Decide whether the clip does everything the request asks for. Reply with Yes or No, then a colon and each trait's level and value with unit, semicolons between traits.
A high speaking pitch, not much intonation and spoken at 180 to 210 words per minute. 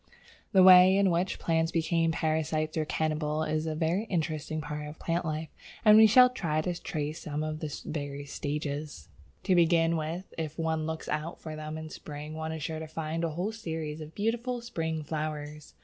No: medium, 160 Hz; narrow, 1.7 semitones; average, 195 wpm